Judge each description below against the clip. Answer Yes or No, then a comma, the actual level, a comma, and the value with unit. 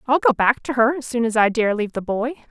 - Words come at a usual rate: No, fast, 310 wpm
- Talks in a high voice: Yes, high, 235 Hz